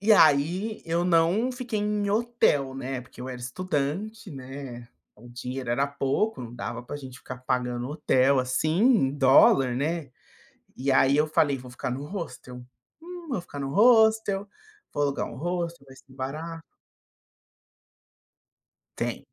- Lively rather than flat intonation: Yes, wide, 7.0 semitones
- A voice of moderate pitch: Yes, medium, 145 Hz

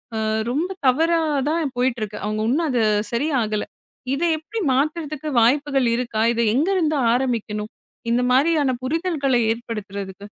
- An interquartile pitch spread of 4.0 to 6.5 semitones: Yes, average, 5.0 semitones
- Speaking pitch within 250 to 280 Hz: Yes, very high, 260 Hz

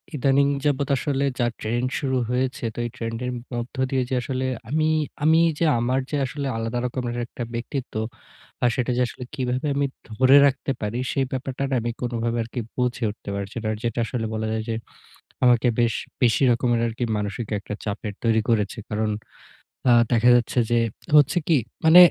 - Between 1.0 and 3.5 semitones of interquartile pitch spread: Yes, narrow, 2.6 semitones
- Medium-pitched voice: No, low, 125 Hz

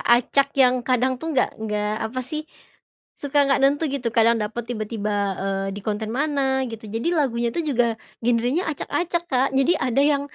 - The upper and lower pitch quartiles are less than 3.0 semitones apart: No, average, 3.8 semitones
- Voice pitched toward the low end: No, very high, 250 Hz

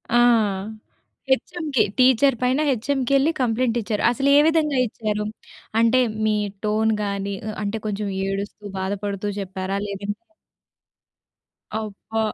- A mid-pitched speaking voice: No, high, 220 Hz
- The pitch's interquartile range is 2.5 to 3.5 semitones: No, average, 4.3 semitones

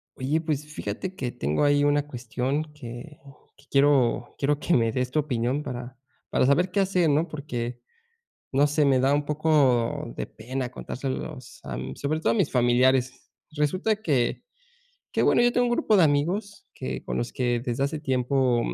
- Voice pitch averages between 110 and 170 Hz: Yes, medium, 140 Hz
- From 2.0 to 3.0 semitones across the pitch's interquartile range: No, average, 3.7 semitones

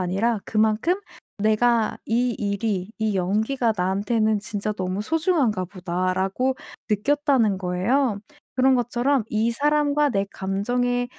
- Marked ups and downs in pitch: No, average, 4.1 semitones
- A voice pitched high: Yes, high, 220 Hz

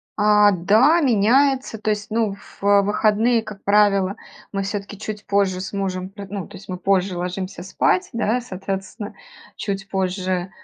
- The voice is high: Yes, high, 200 Hz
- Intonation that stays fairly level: Yes, narrow, 1.9 semitones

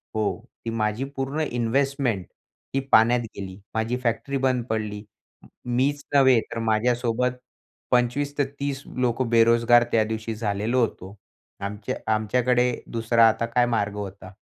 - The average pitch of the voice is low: Yes, low, 115 Hz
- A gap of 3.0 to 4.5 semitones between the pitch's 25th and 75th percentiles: No, narrow, 2.5 semitones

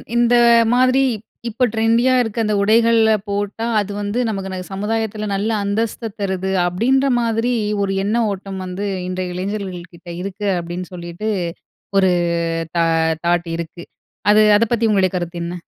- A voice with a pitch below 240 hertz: Yes, high, 200 Hz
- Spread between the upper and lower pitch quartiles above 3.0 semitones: Yes, average, 3.6 semitones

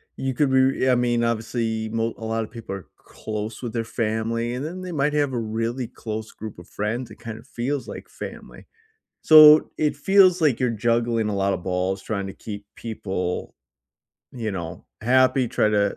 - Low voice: Yes, low, 115 Hz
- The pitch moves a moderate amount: Yes, average, 3.2 semitones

